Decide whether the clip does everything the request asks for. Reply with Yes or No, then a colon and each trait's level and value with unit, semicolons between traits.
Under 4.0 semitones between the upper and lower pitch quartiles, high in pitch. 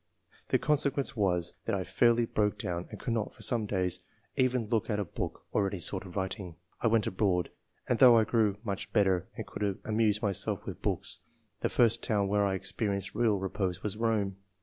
No: average, 3.0 semitones; low, 105 Hz